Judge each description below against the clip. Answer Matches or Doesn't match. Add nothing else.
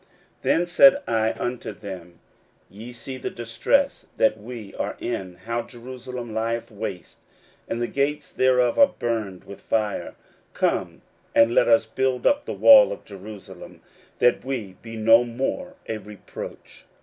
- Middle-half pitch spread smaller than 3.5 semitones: Matches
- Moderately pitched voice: Doesn't match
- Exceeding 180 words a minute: Doesn't match